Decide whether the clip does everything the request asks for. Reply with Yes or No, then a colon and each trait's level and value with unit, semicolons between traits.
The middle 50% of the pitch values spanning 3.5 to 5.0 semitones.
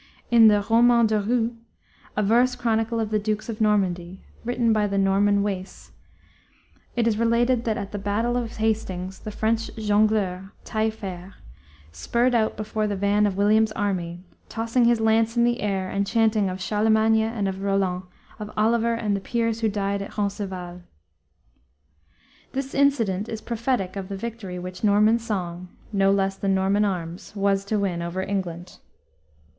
No: average, 2.7 semitones